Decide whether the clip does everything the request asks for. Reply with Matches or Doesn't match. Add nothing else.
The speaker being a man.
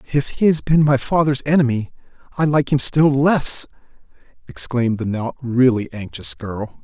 Matches